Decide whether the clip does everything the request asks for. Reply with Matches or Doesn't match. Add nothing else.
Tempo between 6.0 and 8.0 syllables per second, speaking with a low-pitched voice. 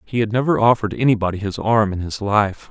Matches